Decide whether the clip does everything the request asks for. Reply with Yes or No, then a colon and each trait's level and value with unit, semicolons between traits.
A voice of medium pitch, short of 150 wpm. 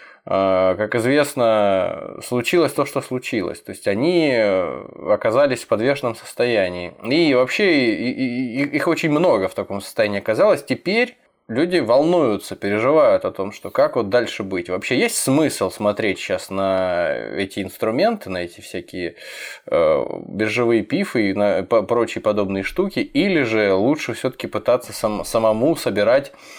No: low, 120 Hz; average, 130 wpm